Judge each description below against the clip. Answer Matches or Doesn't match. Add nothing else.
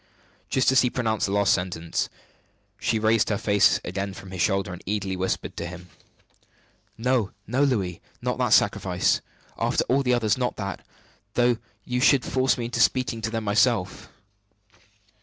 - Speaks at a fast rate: Doesn't match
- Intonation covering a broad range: Doesn't match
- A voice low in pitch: Matches